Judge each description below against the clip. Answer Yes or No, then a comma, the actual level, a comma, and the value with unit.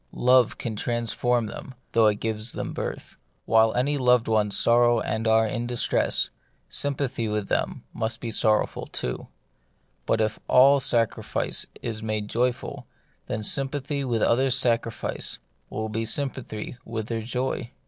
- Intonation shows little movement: Yes, narrow, 2.3 semitones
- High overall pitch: No, low, 115 Hz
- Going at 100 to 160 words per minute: Yes, average, 150 wpm